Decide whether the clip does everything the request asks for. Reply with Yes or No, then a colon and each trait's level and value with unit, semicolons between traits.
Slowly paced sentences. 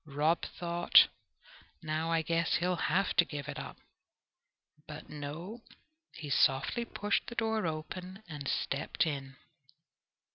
Yes: slow, 130 wpm